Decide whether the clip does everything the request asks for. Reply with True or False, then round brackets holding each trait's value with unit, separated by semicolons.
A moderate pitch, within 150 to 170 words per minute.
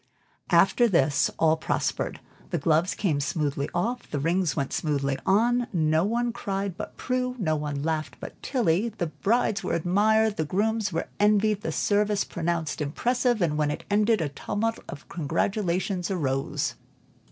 True (180 Hz; 155 wpm)